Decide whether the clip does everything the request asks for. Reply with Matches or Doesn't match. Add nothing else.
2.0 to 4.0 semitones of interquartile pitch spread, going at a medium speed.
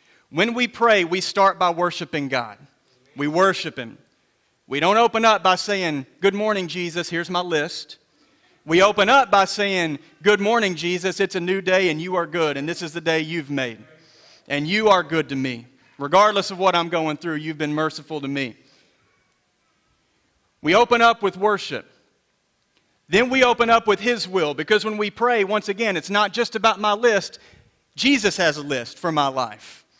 Doesn't match